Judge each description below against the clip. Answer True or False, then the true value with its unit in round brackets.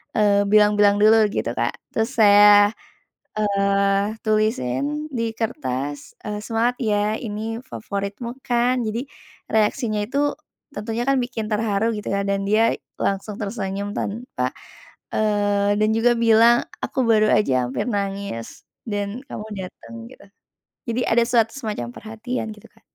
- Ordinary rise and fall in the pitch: False (2.2 semitones)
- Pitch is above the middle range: True (210 Hz)